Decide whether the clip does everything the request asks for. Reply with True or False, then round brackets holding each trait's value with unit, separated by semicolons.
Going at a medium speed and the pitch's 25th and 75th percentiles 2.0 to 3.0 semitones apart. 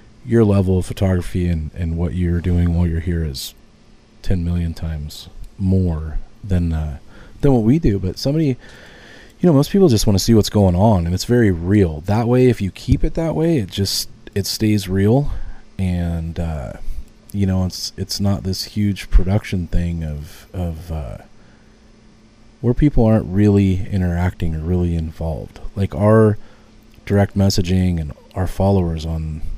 False (170 wpm; 4.1 semitones)